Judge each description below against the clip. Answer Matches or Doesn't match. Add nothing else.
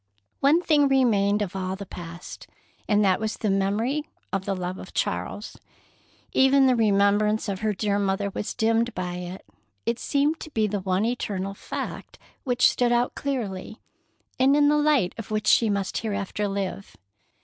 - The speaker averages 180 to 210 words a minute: Doesn't match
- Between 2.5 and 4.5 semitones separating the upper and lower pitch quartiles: Matches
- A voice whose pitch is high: Matches